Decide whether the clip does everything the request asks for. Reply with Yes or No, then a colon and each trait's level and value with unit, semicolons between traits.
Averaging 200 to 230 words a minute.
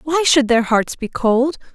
Yes: fast, 205 wpm